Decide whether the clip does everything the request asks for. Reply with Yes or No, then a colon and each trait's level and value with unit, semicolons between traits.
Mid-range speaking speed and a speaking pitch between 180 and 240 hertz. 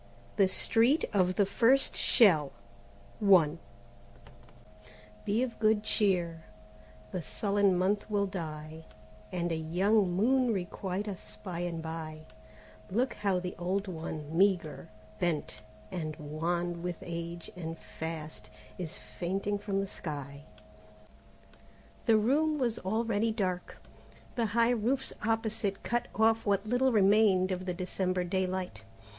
No: slow, 125 wpm; high, 190 Hz